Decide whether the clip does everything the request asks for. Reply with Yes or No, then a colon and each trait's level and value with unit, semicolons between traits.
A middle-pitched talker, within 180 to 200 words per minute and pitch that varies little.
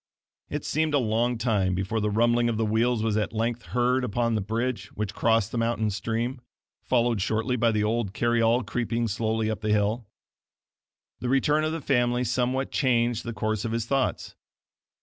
No: low, 115 Hz; average, 190 wpm; narrow, 2.0 semitones